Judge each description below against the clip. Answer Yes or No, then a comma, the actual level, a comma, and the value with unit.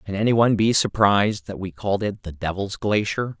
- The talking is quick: No, average, 195 wpm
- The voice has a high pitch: No, low, 100 Hz